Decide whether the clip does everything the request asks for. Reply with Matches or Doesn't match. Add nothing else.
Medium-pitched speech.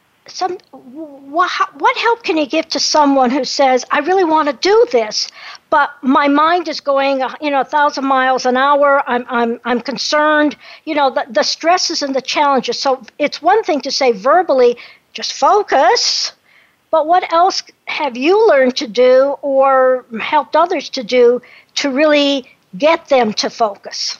Doesn't match